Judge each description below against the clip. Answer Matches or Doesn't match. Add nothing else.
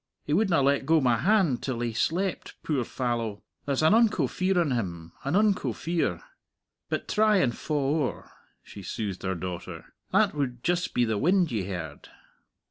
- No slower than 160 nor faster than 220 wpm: Matches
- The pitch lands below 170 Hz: Matches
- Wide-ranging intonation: Matches